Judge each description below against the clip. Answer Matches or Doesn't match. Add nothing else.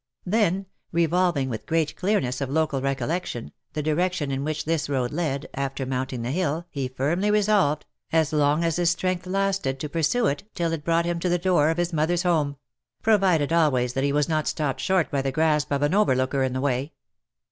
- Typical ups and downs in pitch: Matches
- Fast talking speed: Matches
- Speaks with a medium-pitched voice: Matches